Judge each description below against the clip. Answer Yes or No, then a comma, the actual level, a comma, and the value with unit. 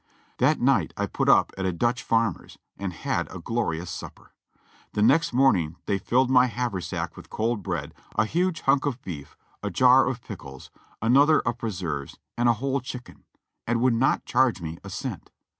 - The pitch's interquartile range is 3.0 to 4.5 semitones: No, wide, 5.4 semitones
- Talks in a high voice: No, low, 115 Hz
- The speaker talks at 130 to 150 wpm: No, average, 190 wpm